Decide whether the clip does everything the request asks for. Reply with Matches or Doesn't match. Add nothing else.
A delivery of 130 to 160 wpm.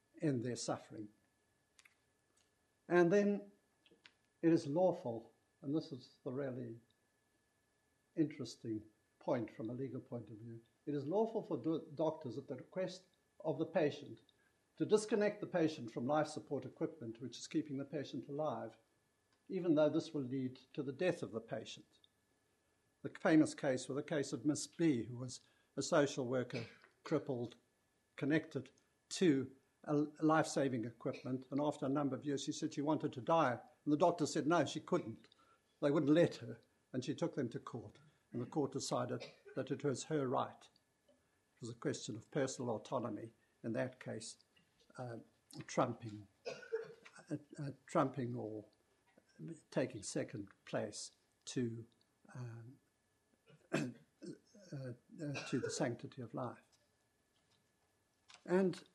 Matches